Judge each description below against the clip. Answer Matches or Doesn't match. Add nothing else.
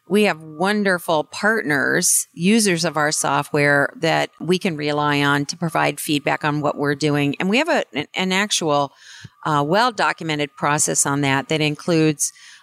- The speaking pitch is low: Doesn't match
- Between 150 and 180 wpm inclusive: Matches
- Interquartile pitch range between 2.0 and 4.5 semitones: Matches